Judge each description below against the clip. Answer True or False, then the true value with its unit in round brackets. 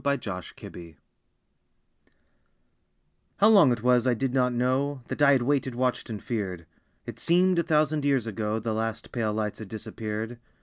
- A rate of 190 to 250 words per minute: False (180 wpm)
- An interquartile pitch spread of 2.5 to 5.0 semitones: True (4.3 semitones)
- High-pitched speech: False (120 Hz)